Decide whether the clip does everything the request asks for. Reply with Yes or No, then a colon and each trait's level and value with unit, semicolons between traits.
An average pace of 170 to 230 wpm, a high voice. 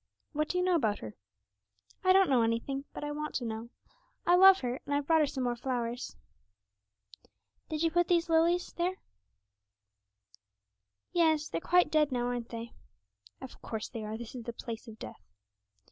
Yes: average, 180 wpm; very high, 275 Hz